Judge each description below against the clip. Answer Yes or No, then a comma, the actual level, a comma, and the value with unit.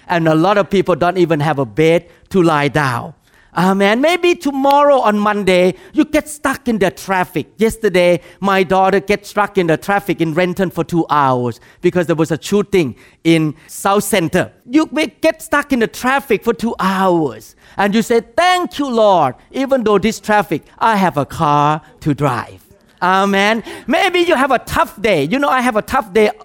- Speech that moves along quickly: No, average, 195 wpm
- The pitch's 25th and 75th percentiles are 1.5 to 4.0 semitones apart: No, wide, 5.6 semitones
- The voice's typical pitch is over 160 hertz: Yes, high, 190 Hz